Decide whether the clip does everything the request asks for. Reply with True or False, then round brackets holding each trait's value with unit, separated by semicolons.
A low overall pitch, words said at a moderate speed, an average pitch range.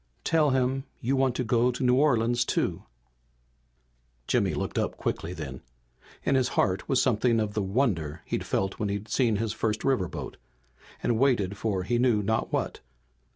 True (115 Hz; 170 wpm; 4.1 semitones)